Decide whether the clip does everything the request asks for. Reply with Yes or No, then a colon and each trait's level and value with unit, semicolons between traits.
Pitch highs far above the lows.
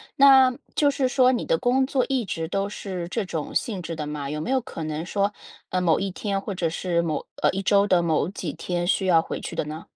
Yes: wide, 5.8 semitones